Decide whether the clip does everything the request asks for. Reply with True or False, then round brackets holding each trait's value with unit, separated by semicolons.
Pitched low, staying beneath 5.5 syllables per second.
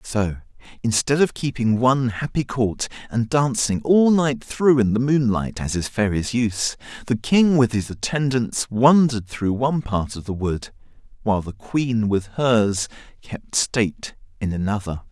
True (120 Hz; 4.4 syllables/s)